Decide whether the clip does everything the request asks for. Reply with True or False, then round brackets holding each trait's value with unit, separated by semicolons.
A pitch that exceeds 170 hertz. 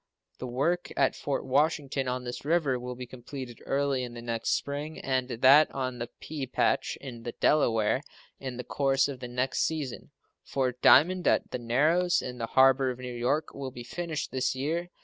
False (130 Hz)